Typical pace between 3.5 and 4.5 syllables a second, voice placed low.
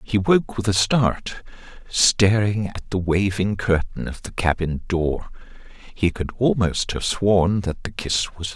Yes: 4.0 syllables/s; very low, 95 Hz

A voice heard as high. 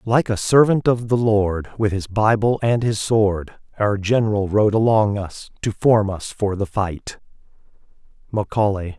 No: low, 105 Hz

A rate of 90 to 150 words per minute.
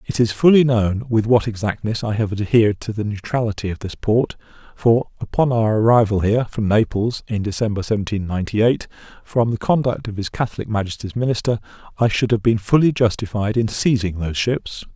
No: average, 185 wpm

